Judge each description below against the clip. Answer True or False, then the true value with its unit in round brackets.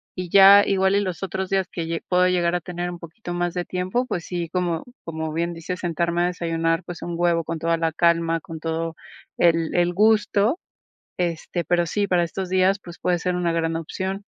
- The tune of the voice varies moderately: False (1.9 semitones)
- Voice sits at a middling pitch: True (175 Hz)